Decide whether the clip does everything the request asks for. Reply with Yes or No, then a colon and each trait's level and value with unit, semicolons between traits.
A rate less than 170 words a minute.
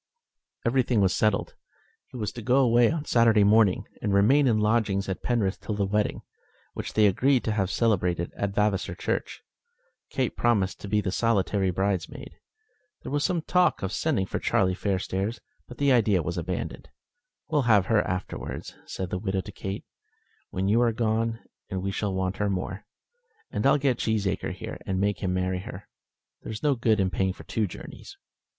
No: average, 185 wpm